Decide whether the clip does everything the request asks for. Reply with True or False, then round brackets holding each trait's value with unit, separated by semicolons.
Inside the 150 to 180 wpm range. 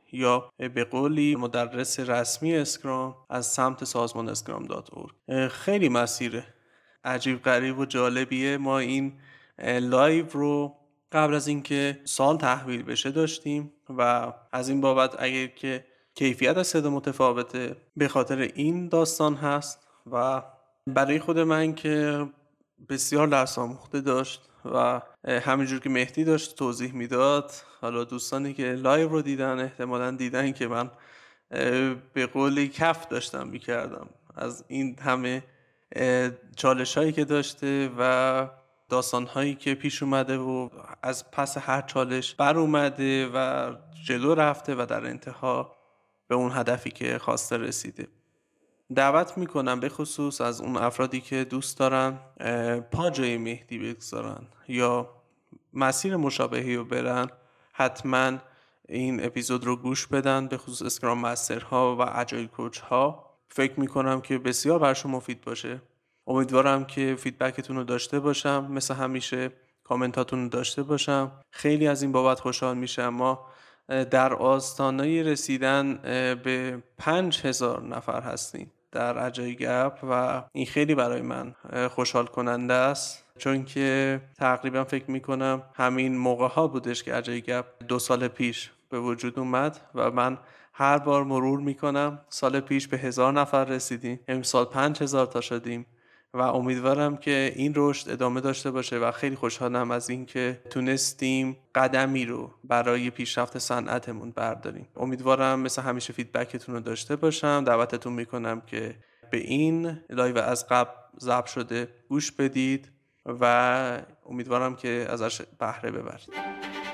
False (135 wpm)